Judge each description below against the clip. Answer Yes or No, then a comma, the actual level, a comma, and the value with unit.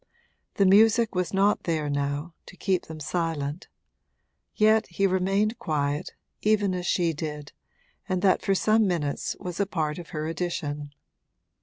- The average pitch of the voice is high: No, medium, 175 Hz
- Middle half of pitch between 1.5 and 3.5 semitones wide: No, average, 4.4 semitones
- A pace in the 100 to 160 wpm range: Yes, average, 150 wpm